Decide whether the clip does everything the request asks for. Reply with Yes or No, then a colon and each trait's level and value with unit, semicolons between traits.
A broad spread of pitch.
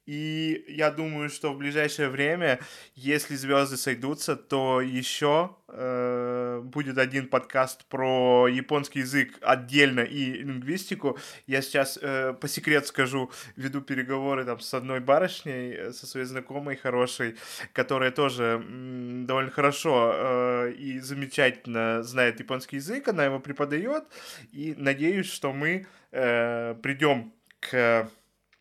No: narrow, 2.4 semitones